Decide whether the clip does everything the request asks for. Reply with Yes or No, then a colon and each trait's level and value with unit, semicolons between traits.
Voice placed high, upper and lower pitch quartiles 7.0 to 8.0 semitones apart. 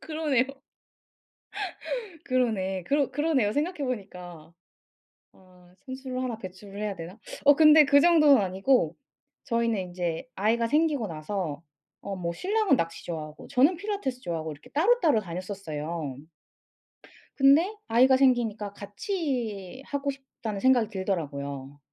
Yes: high, 220 Hz; wide, 7.3 semitones